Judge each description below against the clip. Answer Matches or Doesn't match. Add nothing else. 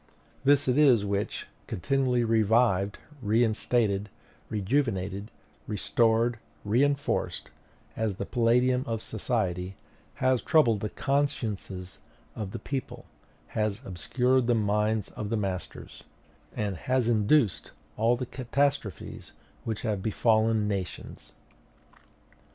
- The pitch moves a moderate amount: Matches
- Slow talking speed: Matches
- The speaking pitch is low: Matches